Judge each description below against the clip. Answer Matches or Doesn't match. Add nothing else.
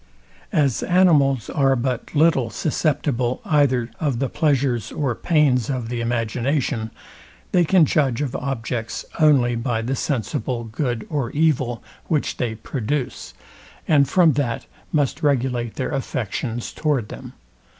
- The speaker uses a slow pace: Matches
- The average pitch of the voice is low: Matches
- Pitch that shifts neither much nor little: Matches